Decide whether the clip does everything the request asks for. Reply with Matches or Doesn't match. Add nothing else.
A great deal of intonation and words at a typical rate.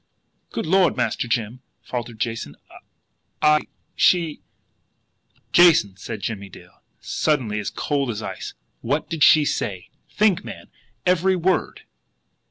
Doesn't match